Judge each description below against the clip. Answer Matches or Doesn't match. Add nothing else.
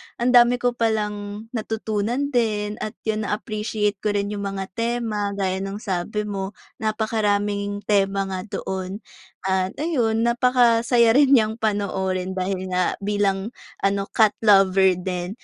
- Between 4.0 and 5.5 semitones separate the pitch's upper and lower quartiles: Doesn't match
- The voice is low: Doesn't match